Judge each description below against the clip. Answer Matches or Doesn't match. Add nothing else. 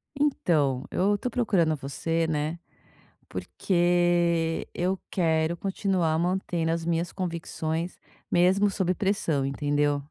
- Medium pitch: Matches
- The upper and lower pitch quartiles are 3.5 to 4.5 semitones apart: Doesn't match